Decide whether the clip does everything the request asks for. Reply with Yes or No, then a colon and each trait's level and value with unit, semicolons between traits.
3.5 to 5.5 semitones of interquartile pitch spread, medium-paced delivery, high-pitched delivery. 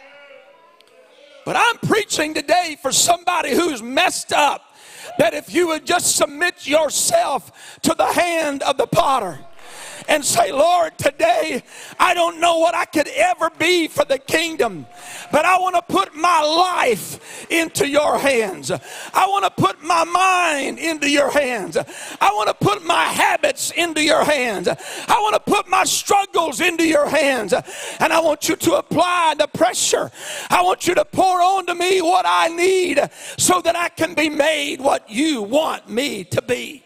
No: average, 3.0 semitones; average, 170 wpm; very high, 330 Hz